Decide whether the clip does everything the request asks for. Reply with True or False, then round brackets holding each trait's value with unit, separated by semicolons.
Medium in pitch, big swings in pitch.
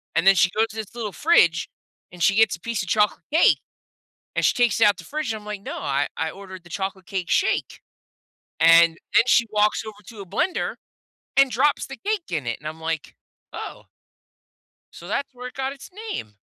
False (210 Hz; 6.0 semitones)